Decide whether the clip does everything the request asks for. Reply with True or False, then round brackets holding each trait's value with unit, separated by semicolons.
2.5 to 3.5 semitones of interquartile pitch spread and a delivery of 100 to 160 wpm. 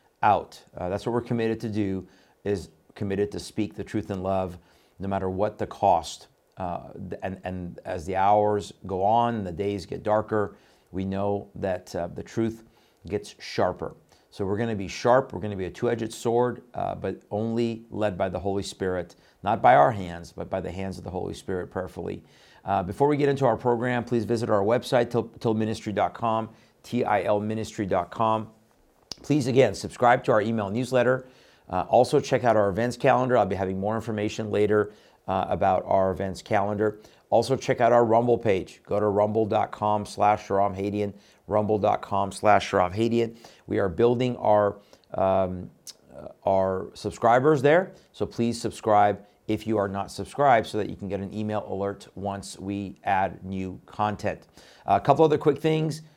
False (2.9 semitones; 175 wpm)